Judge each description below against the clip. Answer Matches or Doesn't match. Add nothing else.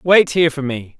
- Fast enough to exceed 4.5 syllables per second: Matches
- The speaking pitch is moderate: Matches